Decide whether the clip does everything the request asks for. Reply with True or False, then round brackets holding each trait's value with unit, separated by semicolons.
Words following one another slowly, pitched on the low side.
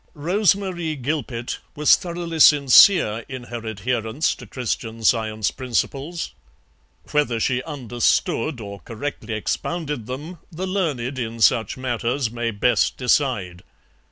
True (120 wpm; 130 Hz)